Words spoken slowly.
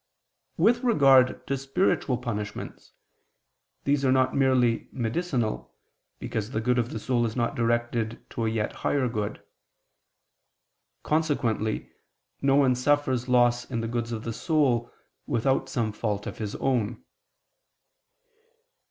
Yes: slow, 130 wpm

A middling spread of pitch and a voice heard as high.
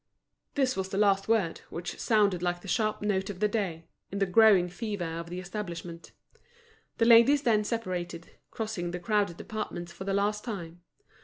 Yes: average, 3.4 semitones; high, 195 Hz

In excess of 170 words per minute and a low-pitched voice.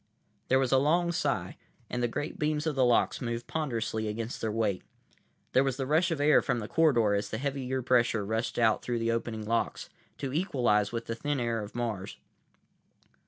Yes: average, 200 wpm; low, 120 Hz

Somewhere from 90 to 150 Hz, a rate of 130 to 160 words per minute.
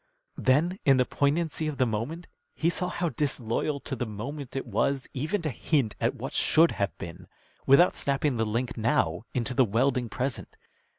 No: low, 135 Hz; average, 180 wpm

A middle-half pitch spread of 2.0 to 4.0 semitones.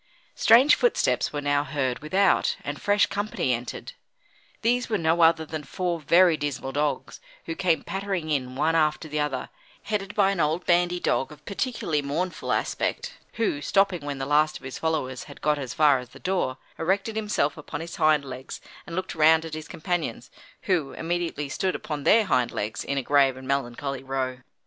No: average, 4.7 semitones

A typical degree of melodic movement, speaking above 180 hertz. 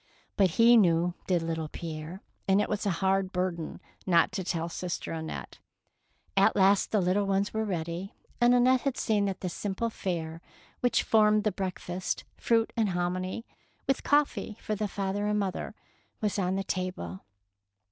Yes: average, 3.2 semitones; high, 190 Hz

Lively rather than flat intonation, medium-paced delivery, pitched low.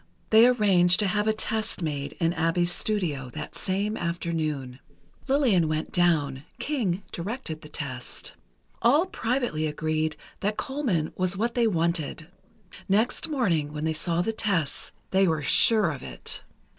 No: wide, 5.7 semitones; average, 145 wpm; medium, 175 Hz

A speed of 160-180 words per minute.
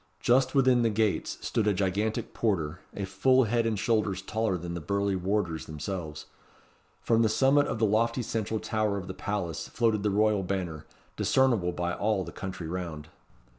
Yes: average, 175 wpm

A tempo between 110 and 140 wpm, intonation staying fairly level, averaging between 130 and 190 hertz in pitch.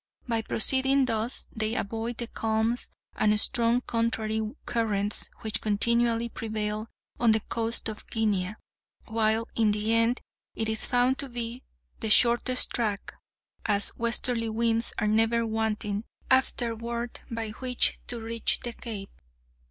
No: slow, 135 wpm; narrow, 1.4 semitones; high, 225 Hz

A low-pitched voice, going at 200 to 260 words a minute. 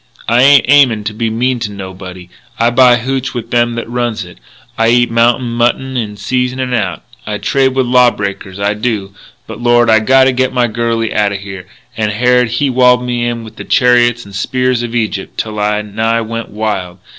Yes: low, 115 Hz; fast, 205 wpm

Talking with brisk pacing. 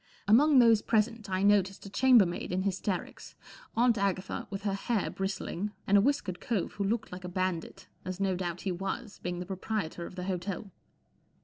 No: average, 185 wpm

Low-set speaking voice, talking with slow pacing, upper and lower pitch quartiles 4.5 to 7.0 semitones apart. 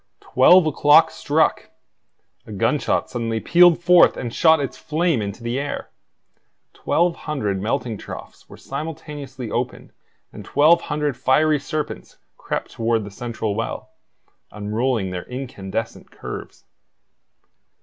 Yes: low, 130 Hz; slow, 120 wpm; wide, 5.5 semitones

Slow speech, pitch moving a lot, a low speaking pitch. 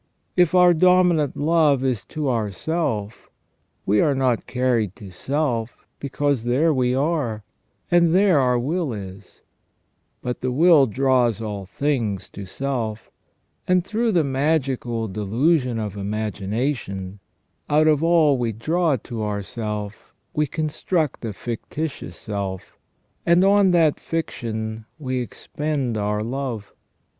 Yes: slow, 125 wpm; wide, 6.1 semitones; low, 130 Hz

